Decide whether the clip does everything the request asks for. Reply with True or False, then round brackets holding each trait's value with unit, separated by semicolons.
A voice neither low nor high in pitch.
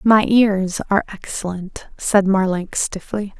False (200 Hz)